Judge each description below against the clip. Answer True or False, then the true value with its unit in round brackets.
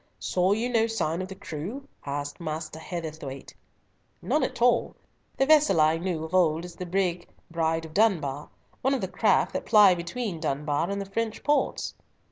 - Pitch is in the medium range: True (180 Hz)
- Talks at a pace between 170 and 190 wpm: True (180 wpm)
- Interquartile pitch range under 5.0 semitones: False (5.4 semitones)